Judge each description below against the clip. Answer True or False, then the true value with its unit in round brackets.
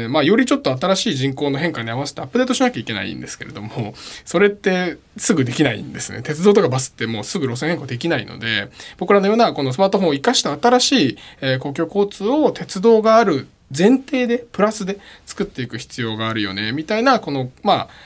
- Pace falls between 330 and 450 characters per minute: False (460 characters per minute)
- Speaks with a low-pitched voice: False (170 Hz)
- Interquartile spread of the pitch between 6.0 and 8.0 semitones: False (8.8 semitones)